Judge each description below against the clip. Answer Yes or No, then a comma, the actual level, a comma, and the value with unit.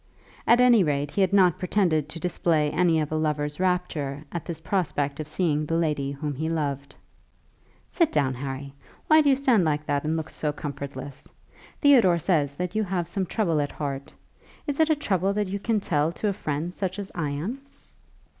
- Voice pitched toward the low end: No, medium, 160 Hz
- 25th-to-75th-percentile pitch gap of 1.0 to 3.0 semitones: No, average, 4.6 semitones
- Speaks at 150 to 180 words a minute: No, average, 200 wpm